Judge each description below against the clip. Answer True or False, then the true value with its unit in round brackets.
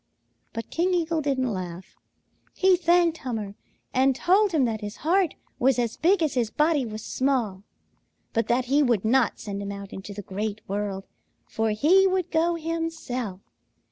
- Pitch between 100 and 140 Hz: False (255 Hz)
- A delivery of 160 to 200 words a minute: True (170 wpm)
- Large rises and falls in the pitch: True (7.6 semitones)